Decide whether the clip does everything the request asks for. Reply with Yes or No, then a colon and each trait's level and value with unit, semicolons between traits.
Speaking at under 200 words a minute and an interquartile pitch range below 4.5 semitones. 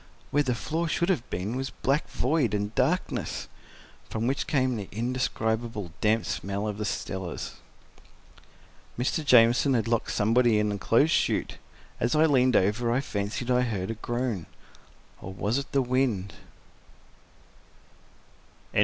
Yes: average, 140 wpm; average, 3.7 semitones